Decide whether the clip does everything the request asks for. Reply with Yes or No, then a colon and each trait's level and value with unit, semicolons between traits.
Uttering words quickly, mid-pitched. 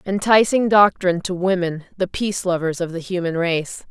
No: average, 170 wpm; medium, 180 Hz